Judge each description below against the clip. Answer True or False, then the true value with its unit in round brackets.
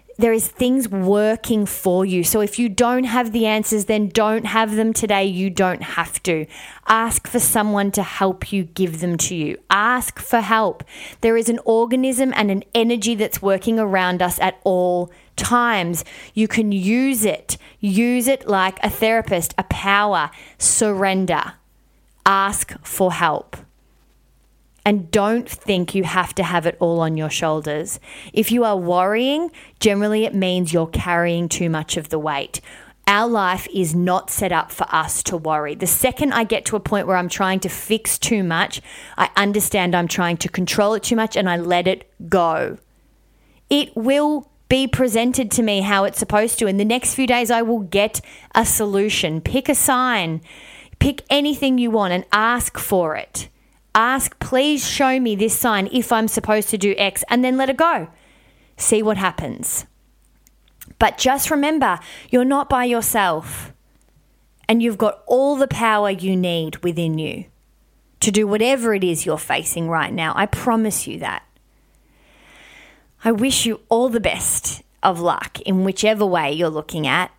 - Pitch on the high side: True (210 Hz)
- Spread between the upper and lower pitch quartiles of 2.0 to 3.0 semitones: False (4.2 semitones)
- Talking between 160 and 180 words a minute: True (175 wpm)